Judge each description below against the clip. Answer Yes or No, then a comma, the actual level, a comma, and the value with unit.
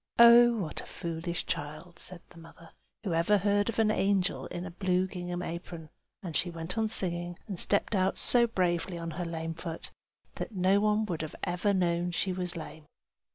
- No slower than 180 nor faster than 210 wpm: Yes, average, 195 wpm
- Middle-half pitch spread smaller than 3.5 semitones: Yes, average, 3.0 semitones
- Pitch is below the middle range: No, medium, 180 Hz